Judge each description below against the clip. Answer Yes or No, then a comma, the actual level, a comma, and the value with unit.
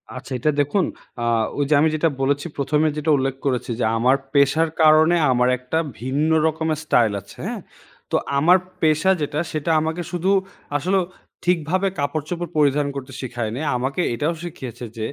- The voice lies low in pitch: No, medium, 150 Hz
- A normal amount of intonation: Yes, average, 3.4 semitones